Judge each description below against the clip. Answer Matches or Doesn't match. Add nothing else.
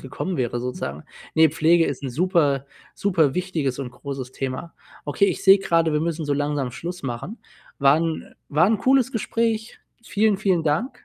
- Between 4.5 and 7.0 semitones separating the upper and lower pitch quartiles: Matches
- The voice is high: Doesn't match